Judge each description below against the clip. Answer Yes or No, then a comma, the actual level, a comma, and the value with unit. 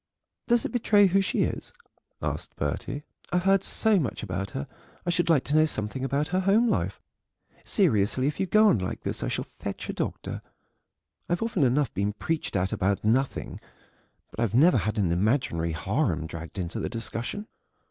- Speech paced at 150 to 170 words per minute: No, average, 185 wpm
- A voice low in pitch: Yes, low, 130 Hz